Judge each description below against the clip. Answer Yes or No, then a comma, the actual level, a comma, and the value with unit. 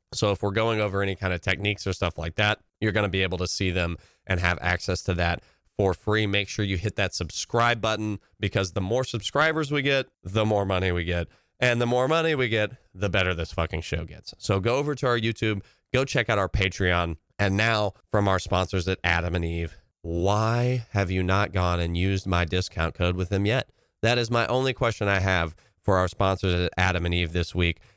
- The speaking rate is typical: No, fast, 230 wpm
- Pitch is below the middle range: Yes, low, 100 Hz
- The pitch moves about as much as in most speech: Yes, average, 3.6 semitones